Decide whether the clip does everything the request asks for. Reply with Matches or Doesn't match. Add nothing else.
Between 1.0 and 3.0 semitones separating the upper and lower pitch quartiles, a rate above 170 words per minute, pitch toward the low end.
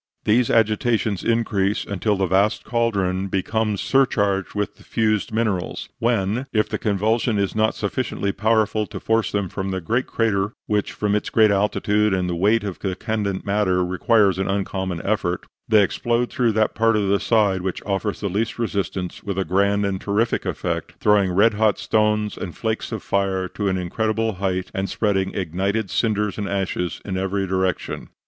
Matches